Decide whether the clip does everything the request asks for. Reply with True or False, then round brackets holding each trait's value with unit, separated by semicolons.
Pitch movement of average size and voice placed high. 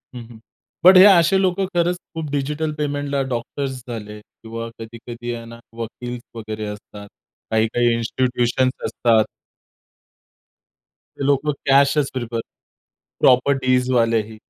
False (3.7 semitones; 125 Hz)